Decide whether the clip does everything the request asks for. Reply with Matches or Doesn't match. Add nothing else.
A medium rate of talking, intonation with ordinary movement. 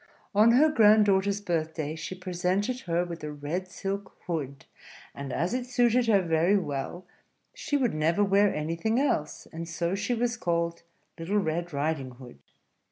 Matches